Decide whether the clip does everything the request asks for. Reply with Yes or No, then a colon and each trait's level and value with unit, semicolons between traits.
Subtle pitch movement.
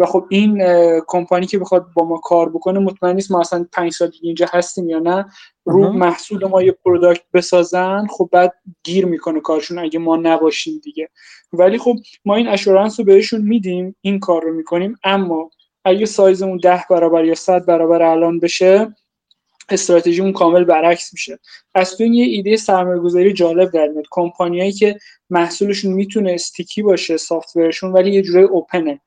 Yes: narrow, 2.3 semitones